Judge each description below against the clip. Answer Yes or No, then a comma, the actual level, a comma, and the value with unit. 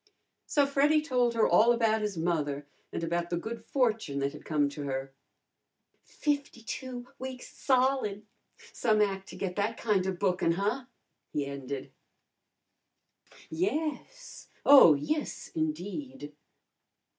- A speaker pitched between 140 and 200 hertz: No, high, 210 Hz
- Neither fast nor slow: No, slow, 125 wpm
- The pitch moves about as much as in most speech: No, wide, 8.1 semitones